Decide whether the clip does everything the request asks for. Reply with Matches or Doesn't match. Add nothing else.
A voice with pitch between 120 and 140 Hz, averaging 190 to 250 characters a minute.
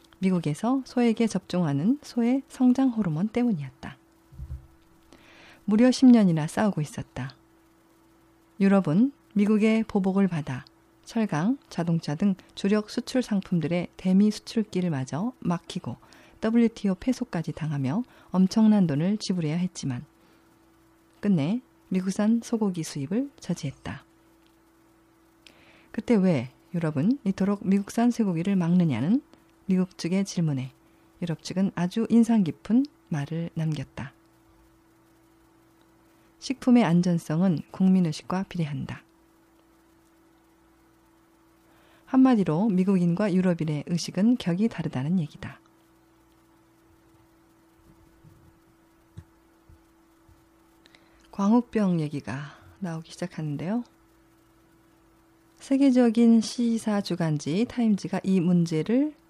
Doesn't match